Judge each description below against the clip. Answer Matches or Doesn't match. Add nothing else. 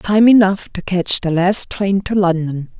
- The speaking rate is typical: Matches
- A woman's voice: Matches